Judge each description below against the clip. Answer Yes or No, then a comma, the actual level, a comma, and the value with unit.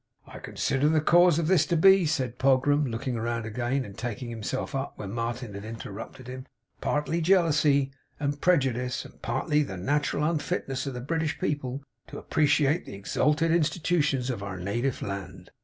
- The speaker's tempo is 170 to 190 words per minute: Yes, average, 180 wpm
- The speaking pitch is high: No, low, 135 Hz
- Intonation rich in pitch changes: No, average, 4.2 semitones